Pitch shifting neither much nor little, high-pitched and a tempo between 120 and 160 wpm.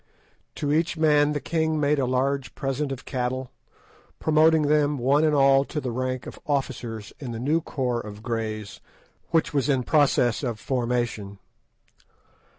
No: average, 3.5 semitones; low, 135 Hz; average, 155 wpm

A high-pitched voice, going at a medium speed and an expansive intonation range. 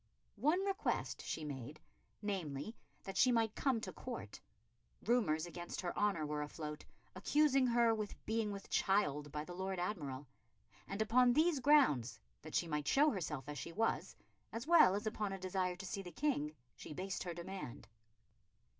Yes: high, 195 Hz; average, 170 wpm; wide, 7.3 semitones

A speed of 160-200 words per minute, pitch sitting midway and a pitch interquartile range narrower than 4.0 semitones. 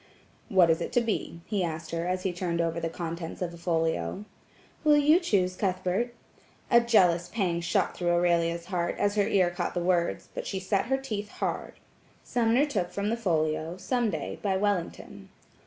Yes: average, 190 wpm; medium, 180 Hz; average, 3.6 semitones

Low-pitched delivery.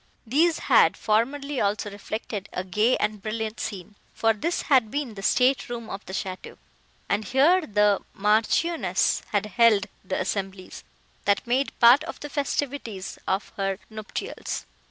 No: high, 220 Hz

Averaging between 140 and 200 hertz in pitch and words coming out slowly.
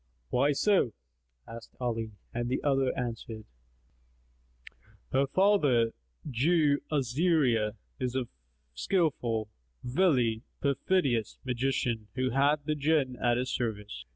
No: low, 130 Hz; slow, 105 wpm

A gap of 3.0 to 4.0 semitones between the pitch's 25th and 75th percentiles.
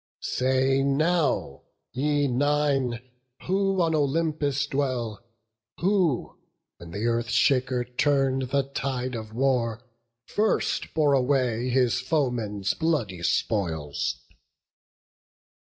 Yes: average, 3.5 semitones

